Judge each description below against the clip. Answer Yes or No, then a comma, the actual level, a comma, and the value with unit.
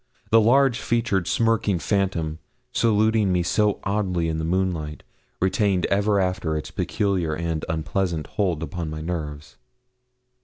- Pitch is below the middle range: Yes, very low, 90 Hz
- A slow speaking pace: Yes, slow, 130 wpm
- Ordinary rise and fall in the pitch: Yes, average, 4.4 semitones